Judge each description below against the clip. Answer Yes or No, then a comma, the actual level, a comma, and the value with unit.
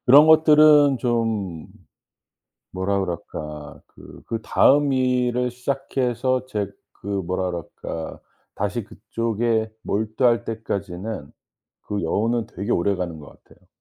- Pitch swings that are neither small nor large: Yes, average, 4.8 semitones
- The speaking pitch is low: Yes, low, 110 Hz